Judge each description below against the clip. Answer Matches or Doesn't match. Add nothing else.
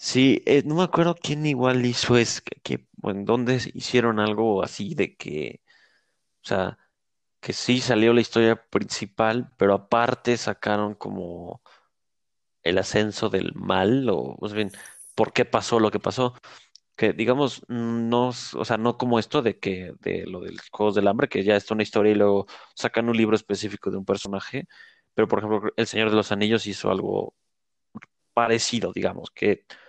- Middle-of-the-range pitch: Doesn't match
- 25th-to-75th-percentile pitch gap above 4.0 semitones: Doesn't match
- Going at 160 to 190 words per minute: Matches